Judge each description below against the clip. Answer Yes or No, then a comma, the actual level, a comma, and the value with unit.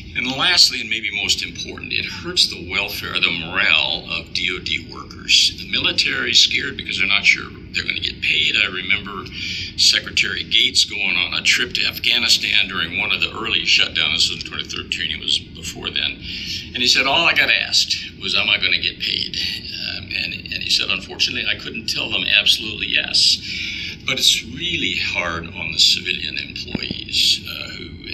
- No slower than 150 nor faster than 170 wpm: No, average, 190 wpm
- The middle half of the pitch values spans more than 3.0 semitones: No, narrow, 2.6 semitones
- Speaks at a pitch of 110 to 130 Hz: No, very low, 90 Hz